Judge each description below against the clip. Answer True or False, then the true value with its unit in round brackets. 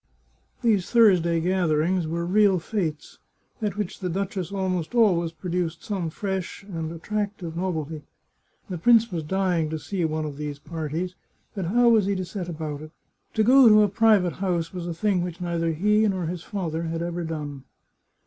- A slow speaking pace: False (180 wpm)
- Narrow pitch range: False (3.5 semitones)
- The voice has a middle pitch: True (180 Hz)